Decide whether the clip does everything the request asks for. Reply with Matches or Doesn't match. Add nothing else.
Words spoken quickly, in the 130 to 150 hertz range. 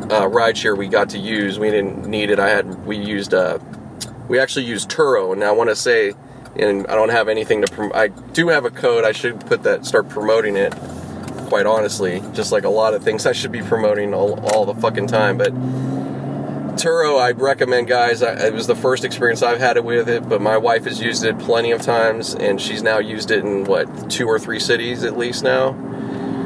Doesn't match